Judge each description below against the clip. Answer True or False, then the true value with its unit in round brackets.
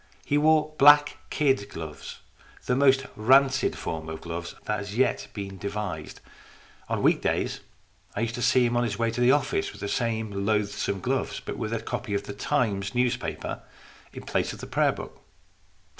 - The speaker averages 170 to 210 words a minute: True (185 wpm)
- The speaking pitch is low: True (115 Hz)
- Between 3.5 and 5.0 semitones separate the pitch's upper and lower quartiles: True (4.6 semitones)